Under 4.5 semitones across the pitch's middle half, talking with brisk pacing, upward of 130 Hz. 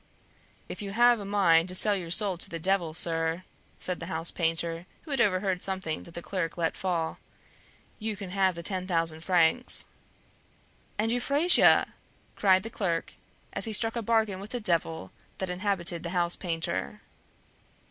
No: average, 3.5 semitones; average, 170 wpm; medium, 185 Hz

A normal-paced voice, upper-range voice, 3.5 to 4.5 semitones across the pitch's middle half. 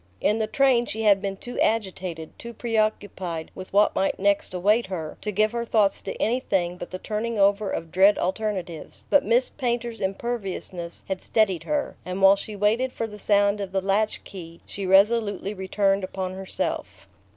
No: average, 180 wpm; high, 200 Hz; average, 2.7 semitones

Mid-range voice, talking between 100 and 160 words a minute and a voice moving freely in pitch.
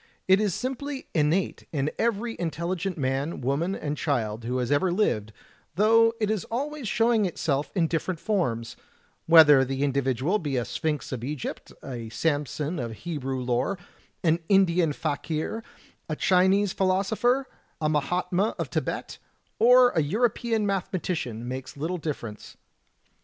Yes: medium, 165 Hz; average, 140 wpm; wide, 6.5 semitones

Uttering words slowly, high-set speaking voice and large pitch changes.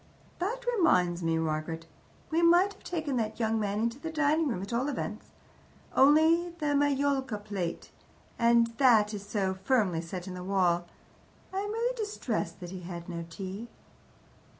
No: average, 165 wpm; high, 230 Hz; wide, 9.0 semitones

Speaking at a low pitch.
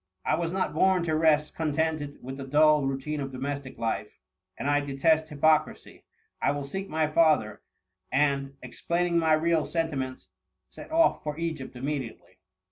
No: medium, 150 Hz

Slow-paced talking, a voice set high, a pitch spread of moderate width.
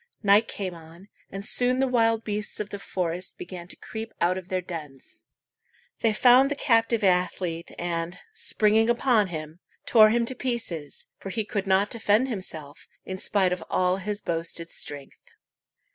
No: average, 165 wpm; high, 195 Hz; average, 4.4 semitones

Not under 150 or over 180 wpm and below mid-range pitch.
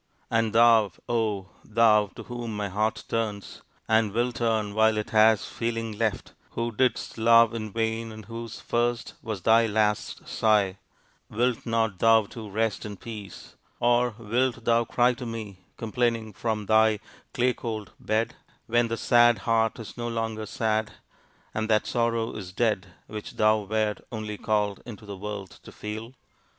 Yes: average, 160 wpm; low, 110 Hz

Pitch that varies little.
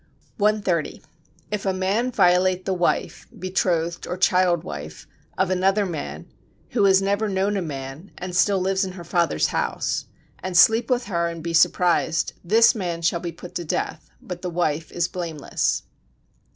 Yes: narrow, 2.3 semitones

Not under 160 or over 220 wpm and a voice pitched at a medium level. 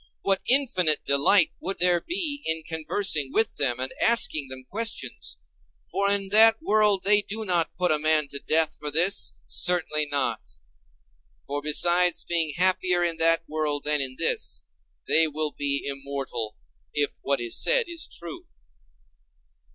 No: average, 150 wpm; medium, 165 Hz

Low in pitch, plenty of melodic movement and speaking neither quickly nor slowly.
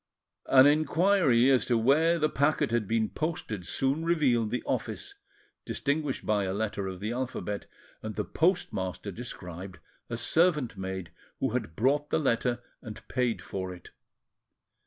Yes: low, 120 Hz; wide, 6.1 semitones; average, 150 wpm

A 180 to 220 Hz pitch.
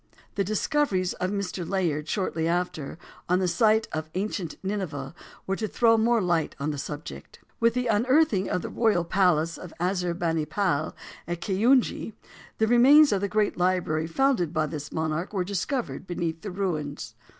Yes: medium, 185 Hz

